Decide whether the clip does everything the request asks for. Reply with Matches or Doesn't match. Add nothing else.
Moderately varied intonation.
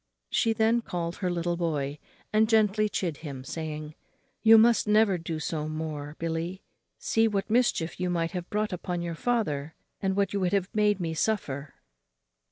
Matches